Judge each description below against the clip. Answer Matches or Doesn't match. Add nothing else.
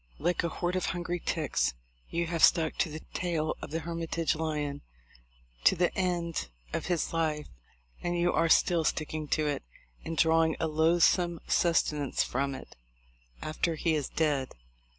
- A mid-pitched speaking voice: Matches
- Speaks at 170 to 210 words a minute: Doesn't match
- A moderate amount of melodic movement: Doesn't match